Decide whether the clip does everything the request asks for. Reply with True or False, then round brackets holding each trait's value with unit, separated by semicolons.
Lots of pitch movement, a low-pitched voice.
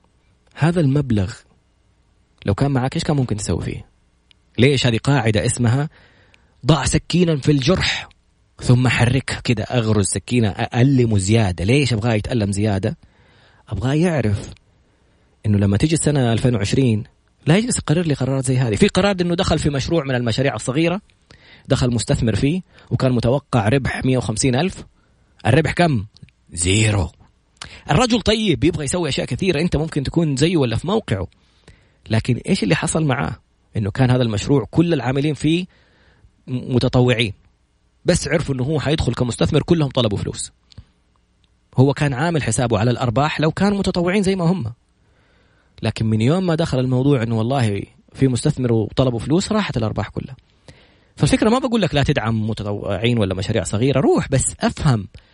True (5.9 semitones; 125 Hz)